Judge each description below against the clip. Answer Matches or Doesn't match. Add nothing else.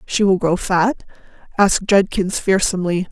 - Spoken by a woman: Matches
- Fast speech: Doesn't match